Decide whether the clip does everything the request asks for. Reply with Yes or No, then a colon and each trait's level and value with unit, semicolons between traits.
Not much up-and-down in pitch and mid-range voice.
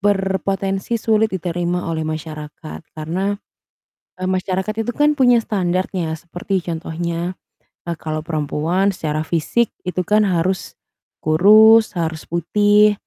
No: average, 3.8 semitones; medium, 180 Hz